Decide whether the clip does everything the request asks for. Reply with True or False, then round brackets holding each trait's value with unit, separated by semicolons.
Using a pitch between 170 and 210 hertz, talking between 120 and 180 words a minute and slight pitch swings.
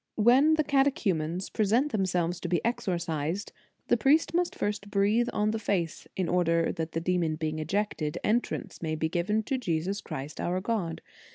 False (190 Hz; 175 wpm; 5.1 semitones)